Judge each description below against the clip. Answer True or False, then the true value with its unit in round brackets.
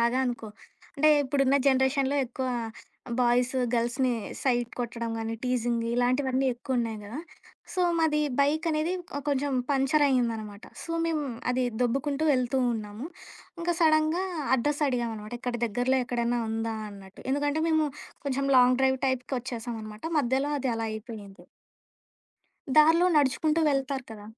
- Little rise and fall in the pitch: False (3.3 semitones)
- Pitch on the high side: True (260 Hz)